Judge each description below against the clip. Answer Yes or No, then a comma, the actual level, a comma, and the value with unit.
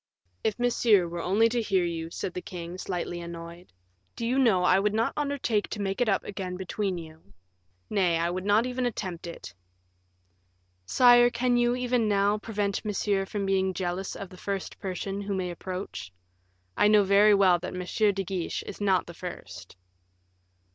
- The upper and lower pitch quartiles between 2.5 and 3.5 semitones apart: Yes, average, 3.0 semitones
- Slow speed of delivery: No, average, 180 wpm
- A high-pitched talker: Yes, high, 195 Hz